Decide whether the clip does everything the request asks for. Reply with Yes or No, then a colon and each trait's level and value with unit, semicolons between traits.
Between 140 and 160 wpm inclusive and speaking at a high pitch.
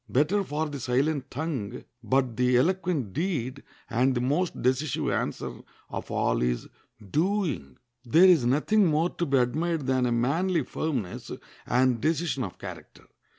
No: average, 150 wpm; medium, 140 Hz